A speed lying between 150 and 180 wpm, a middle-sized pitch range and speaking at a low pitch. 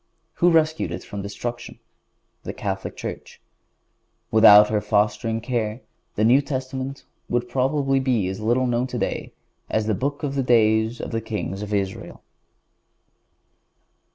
No: average, 140 wpm; average, 3.7 semitones; low, 120 Hz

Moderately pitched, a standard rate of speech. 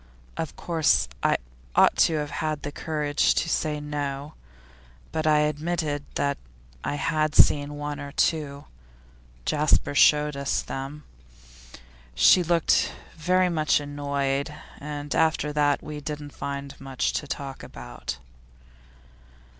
No: medium, 150 Hz; slow, 125 wpm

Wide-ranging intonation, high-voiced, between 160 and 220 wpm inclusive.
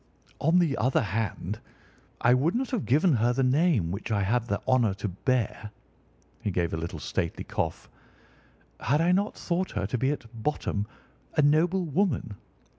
No: wide, 7.2 semitones; low, 125 Hz; average, 165 wpm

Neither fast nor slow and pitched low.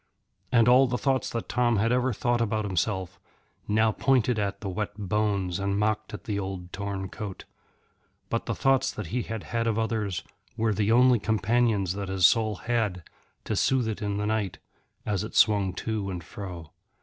Yes: average, 185 wpm; low, 105 Hz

